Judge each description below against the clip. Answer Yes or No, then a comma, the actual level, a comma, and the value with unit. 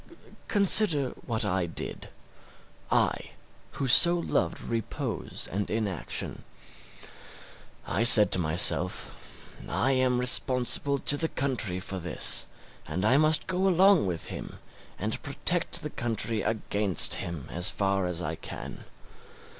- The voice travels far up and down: Yes, wide, 7.2 semitones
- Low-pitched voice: Yes, low, 115 Hz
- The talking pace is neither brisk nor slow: No, slow, 125 wpm